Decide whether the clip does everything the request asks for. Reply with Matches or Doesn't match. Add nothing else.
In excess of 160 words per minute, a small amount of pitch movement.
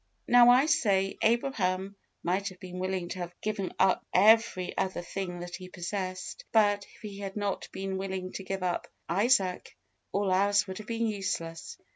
Matches